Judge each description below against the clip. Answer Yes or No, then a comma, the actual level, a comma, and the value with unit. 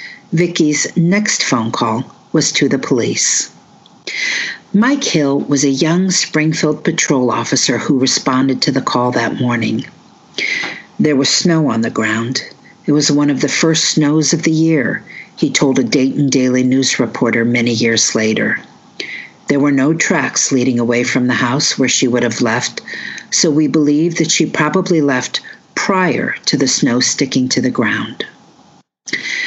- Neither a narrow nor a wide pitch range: Yes, average, 4.3 semitones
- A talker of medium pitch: Yes, medium, 145 Hz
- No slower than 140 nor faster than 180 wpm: Yes, average, 160 wpm